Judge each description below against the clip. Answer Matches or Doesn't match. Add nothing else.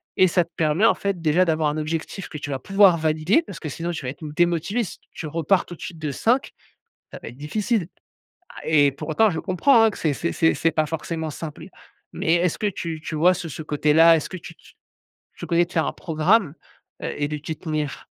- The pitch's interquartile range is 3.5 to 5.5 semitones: Doesn't match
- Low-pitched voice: Doesn't match